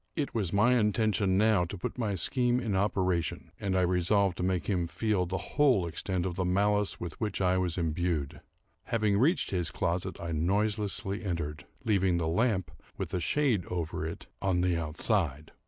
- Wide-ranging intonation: No, average, 3.4 semitones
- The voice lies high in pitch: No, very low, 95 Hz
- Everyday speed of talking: Yes, average, 180 wpm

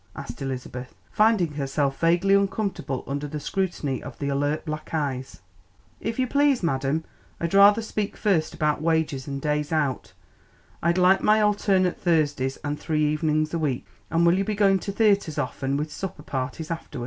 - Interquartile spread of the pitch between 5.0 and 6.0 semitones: Yes, average, 5.3 semitones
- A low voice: No, medium, 155 Hz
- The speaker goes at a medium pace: Yes, average, 170 wpm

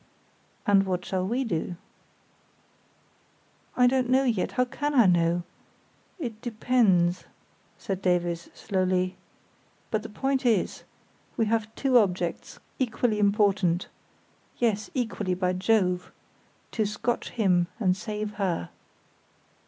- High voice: Yes, high, 210 Hz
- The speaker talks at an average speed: No, slow, 115 wpm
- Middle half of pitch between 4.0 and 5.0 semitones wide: Yes, average, 4.5 semitones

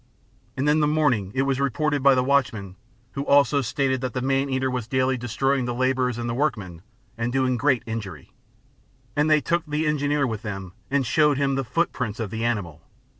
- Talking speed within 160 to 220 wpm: Yes, average, 195 wpm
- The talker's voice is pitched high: No, low, 130 Hz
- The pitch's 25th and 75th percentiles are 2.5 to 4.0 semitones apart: Yes, average, 3.2 semitones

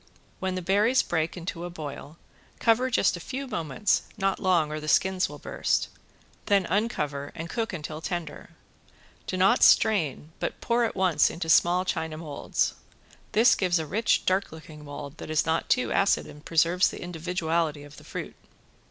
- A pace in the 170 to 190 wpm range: Yes, average, 175 wpm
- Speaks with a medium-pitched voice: Yes, medium, 175 Hz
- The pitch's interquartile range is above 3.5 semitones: Yes, average, 3.9 semitones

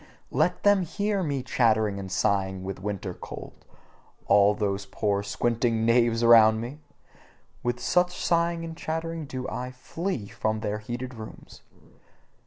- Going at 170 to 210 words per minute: No, average, 140 wpm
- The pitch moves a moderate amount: No, wide, 6.8 semitones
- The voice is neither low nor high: No, low, 115 Hz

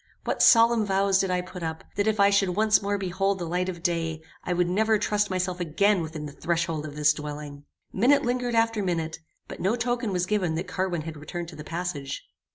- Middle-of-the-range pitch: Yes, medium, 180 Hz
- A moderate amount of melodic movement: Yes, average, 3.8 semitones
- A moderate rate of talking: No, fast, 220 wpm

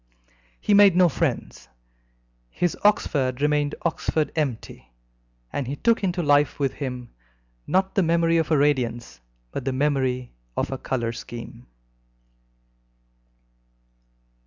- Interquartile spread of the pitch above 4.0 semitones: Yes, average, 4.7 semitones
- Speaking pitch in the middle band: Yes, medium, 145 Hz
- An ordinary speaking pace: No, slow, 120 wpm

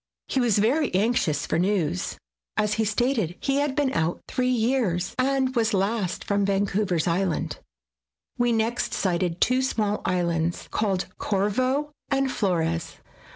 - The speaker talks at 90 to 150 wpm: Yes, average, 145 wpm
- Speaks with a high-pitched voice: Yes, high, 210 Hz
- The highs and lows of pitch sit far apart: Yes, wide, 5.8 semitones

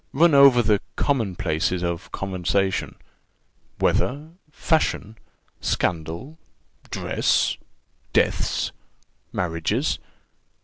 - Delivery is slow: Yes, slow, 75 wpm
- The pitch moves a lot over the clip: Yes, wide, 7.7 semitones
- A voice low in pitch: Yes, low, 105 Hz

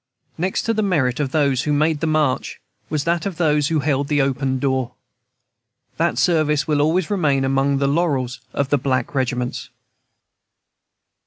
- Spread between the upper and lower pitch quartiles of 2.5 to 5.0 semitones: Yes, average, 2.9 semitones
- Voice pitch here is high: No, medium, 145 Hz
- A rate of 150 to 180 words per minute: Yes, average, 165 wpm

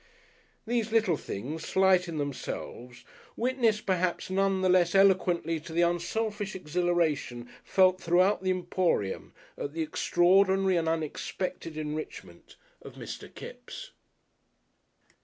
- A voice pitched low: No, medium, 180 Hz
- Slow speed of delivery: Yes, slow, 115 wpm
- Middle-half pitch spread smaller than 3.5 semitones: Yes, average, 3.1 semitones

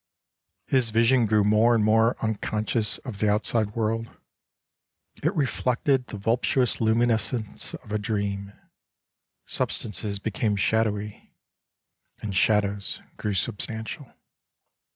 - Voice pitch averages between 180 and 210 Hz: No, low, 110 Hz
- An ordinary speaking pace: No, slow, 110 wpm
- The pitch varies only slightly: Yes, narrow, 2.0 semitones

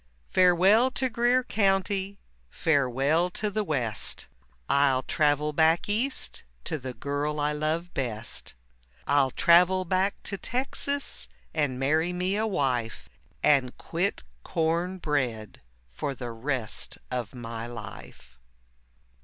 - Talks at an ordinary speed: No, slow, 120 wpm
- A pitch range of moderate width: No, wide, 6.5 semitones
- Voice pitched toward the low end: No, medium, 155 Hz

